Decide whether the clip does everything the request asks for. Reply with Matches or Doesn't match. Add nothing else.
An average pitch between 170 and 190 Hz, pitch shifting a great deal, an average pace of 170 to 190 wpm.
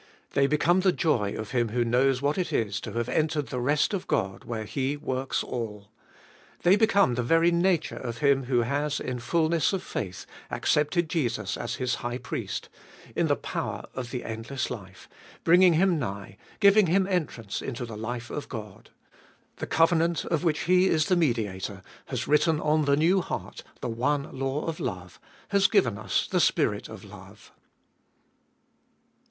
Doesn't match